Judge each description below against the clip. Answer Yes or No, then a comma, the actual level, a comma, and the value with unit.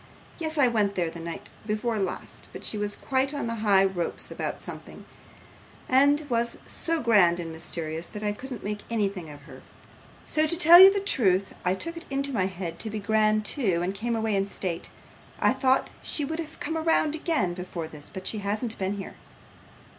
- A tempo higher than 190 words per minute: Yes, average, 200 wpm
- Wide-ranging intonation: Yes, wide, 6.5 semitones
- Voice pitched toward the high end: Yes, high, 215 Hz